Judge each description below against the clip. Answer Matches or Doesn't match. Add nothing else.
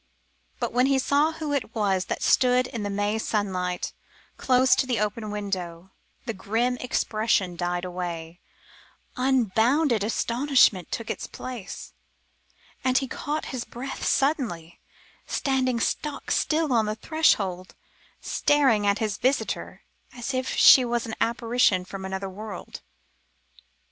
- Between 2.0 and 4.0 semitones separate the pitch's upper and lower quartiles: Doesn't match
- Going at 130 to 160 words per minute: Matches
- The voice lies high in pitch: Matches